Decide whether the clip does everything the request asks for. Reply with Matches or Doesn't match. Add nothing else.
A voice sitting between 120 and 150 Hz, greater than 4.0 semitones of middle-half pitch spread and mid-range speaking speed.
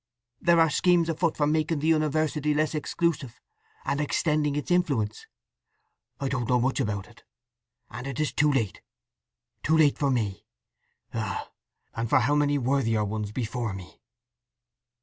Matches